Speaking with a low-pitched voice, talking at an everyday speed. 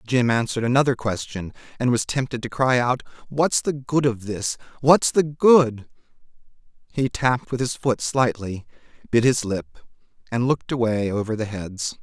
Yes: low, 120 Hz; average, 165 wpm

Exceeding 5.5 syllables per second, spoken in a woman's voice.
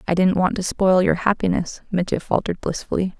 Yes: 5.8 syllables/s; female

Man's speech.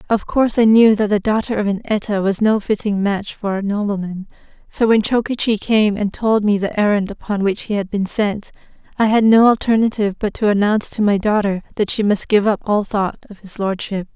No: female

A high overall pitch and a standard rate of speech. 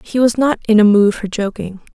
No: high, 215 Hz; fast, 245 wpm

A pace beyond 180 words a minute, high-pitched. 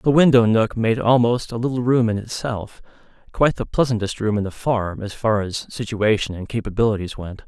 No: average, 195 wpm; low, 115 Hz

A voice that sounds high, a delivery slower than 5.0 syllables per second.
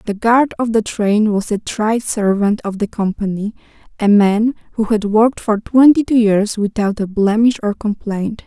Yes: high, 215 Hz; 4.5 syllables/s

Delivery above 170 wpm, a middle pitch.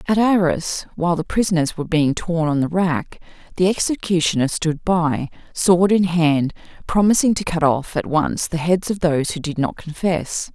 Yes: average, 180 wpm; medium, 170 Hz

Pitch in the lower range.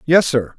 No: medium, 145 Hz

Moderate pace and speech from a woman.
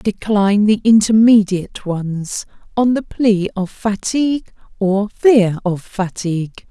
No: slow, 115 wpm; female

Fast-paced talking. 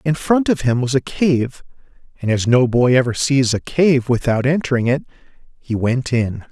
No: average, 195 wpm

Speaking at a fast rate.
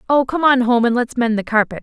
Yes: fast, 295 wpm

